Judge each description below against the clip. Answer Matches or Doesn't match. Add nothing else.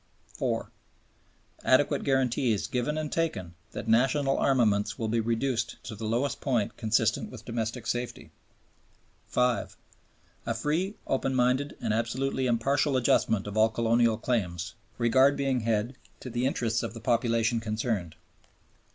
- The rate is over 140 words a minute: Doesn't match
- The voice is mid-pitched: Doesn't match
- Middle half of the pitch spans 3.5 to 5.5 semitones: Doesn't match